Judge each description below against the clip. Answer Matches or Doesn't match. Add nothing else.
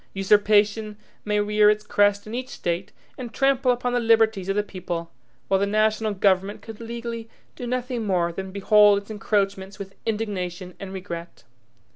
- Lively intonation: Doesn't match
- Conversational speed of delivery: Matches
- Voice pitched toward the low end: Doesn't match